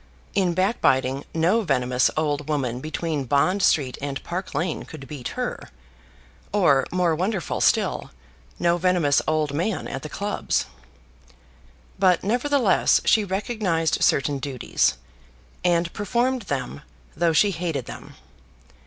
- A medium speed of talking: No, slow, 125 wpm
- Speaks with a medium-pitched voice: Yes, medium, 165 Hz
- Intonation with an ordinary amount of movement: Yes, average, 5.0 semitones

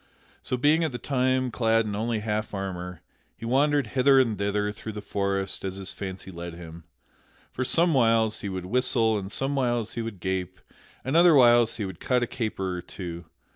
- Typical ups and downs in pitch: Yes, average, 4.7 semitones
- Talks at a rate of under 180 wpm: No, average, 185 wpm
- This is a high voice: No, low, 110 Hz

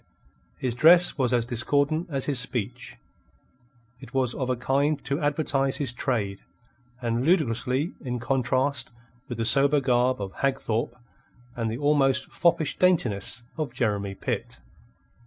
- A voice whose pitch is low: Yes, low, 130 Hz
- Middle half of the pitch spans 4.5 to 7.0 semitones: No, average, 3.1 semitones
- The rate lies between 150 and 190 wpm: No, average, 140 wpm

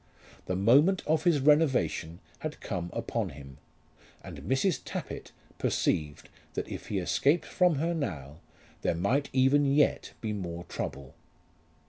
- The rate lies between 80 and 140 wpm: Yes, slow, 135 wpm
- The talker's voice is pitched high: No, low, 130 Hz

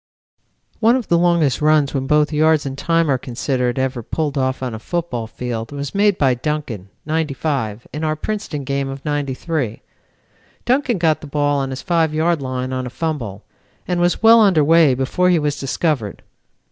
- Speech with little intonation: No, average, 3.9 semitones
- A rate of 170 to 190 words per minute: Yes, average, 185 wpm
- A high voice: No, medium, 145 Hz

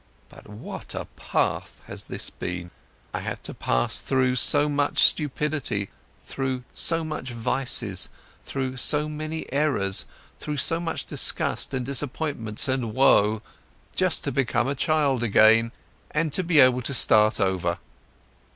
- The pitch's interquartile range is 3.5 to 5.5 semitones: Yes, average, 5.0 semitones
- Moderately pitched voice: No, low, 130 Hz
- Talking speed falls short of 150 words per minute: Yes, average, 140 wpm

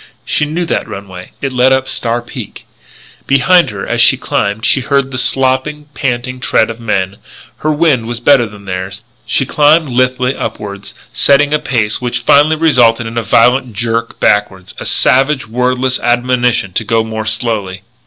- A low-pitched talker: Yes, low, 125 Hz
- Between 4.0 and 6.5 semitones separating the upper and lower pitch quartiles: No, average, 3.5 semitones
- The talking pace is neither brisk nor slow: Yes, average, 170 wpm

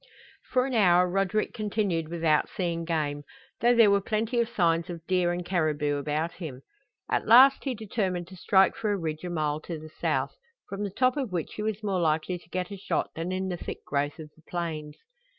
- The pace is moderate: No, fast, 215 wpm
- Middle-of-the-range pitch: Yes, medium, 180 Hz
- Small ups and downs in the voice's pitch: No, average, 4.3 semitones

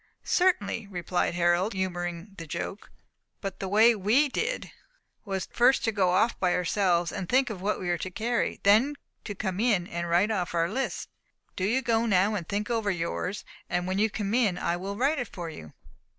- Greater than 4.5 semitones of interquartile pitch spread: No, average, 4.1 semitones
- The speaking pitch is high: Yes, high, 195 Hz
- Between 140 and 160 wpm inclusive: No, average, 200 wpm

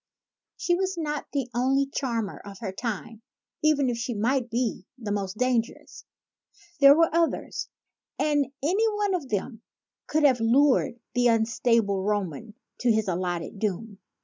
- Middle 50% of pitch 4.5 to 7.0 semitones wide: Yes, average, 5.1 semitones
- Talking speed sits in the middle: Yes, average, 150 wpm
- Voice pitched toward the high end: Yes, high, 240 Hz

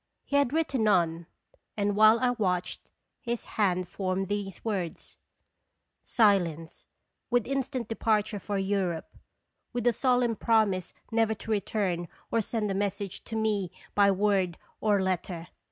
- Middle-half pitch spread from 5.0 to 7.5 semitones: No, average, 3.3 semitones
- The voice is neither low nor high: No, high, 205 Hz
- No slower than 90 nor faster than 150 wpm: Yes, average, 140 wpm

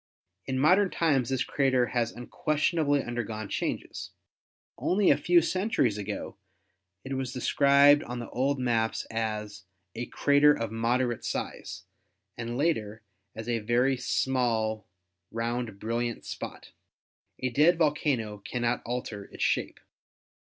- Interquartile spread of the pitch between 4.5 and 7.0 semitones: No, average, 3.8 semitones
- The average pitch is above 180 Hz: No, low, 125 Hz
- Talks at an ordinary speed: No, slow, 125 wpm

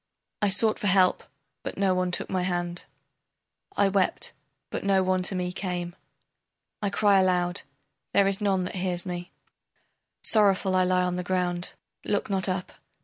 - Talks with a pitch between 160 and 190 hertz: Yes, medium, 185 Hz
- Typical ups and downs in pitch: No, narrow, 1.5 semitones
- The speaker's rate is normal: Yes, average, 165 wpm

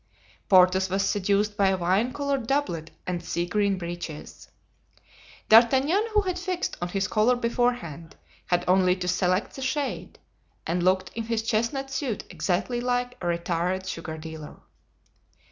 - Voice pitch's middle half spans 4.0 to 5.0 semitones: No, wide, 5.5 semitones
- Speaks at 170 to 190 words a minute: No, average, 145 wpm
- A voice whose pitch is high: Yes, high, 195 Hz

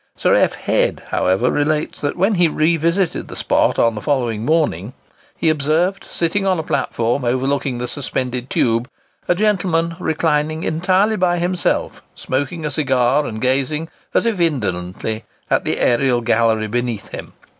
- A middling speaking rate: Yes, average, 155 wpm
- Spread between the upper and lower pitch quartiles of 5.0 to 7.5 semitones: Yes, wide, 5.6 semitones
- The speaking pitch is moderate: Yes, medium, 145 Hz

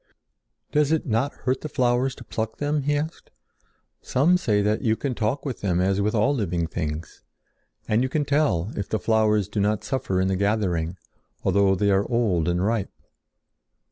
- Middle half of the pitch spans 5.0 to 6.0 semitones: Yes, wide, 5.5 semitones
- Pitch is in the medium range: No, low, 110 Hz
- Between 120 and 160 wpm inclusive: No, average, 185 wpm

